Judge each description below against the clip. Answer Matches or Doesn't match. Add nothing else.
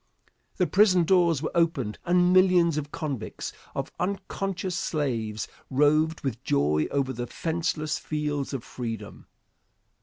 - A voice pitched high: Doesn't match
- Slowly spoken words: Matches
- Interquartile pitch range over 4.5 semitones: Matches